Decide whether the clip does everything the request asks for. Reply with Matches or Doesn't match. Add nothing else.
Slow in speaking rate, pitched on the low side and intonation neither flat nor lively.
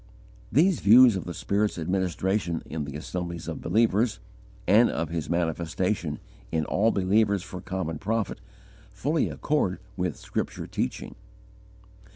Matches